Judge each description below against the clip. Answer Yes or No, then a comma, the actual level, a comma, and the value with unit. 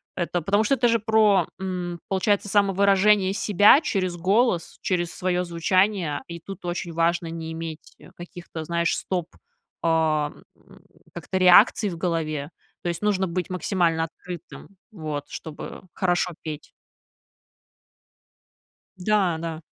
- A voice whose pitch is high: No, medium, 180 Hz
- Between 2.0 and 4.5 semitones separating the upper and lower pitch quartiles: Yes, average, 2.9 semitones